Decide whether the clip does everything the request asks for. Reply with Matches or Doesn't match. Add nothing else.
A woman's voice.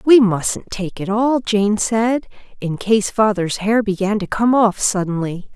Matches